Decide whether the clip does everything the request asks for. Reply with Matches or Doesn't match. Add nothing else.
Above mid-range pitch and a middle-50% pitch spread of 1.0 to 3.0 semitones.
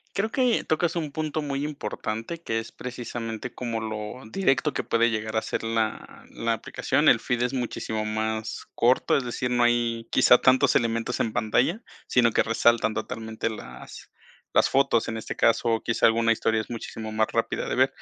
Doesn't match